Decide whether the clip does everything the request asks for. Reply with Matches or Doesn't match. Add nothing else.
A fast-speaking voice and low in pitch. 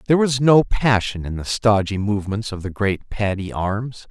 Doesn't match